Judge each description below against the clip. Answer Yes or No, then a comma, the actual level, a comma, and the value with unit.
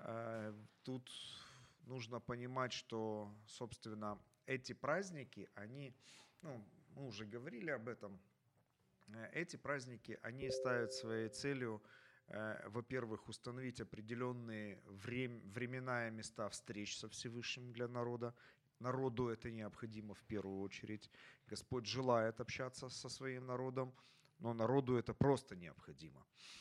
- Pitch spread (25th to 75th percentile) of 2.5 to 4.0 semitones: Yes, average, 2.8 semitones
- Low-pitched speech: Yes, low, 120 Hz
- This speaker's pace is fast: No, average, 115 wpm